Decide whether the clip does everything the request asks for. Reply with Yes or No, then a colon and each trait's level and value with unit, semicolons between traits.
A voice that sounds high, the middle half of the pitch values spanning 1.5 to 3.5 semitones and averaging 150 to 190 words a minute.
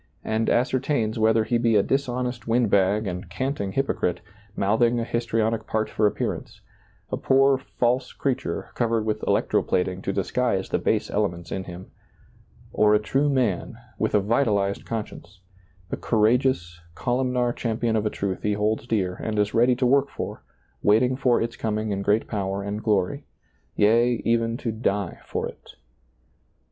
No: low, 110 Hz; average, 3.2 semitones; average, 170 wpm